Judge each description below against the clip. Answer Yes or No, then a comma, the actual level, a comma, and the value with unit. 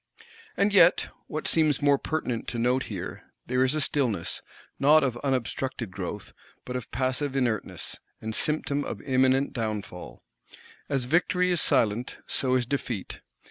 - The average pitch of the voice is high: No, low, 130 Hz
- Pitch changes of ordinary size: Yes, average, 3.5 semitones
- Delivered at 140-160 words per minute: Yes, average, 145 wpm